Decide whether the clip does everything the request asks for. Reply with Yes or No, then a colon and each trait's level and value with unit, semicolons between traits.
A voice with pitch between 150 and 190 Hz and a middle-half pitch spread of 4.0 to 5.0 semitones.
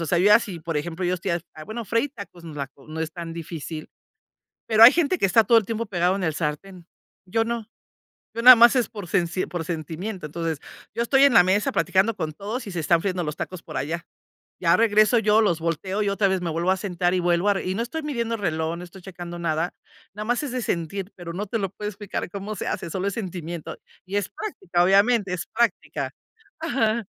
Yes: medium, 185 Hz; average, 4.3 semitones